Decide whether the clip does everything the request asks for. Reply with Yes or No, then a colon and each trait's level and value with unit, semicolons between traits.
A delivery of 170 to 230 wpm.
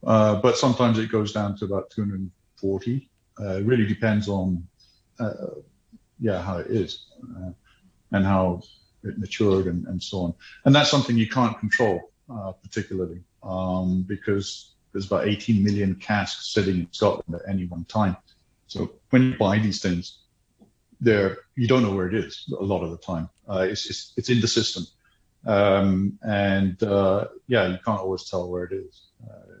Yes: average, 175 wpm